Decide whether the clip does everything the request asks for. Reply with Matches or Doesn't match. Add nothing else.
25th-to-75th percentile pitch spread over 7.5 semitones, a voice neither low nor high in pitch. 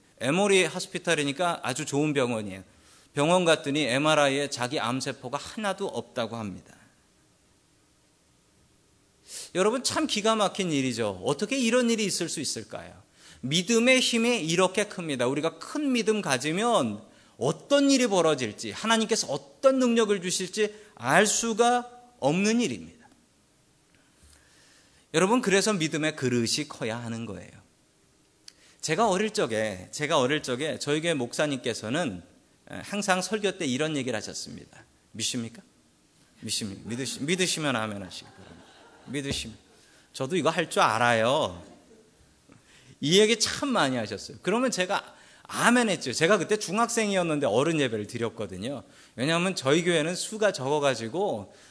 Matches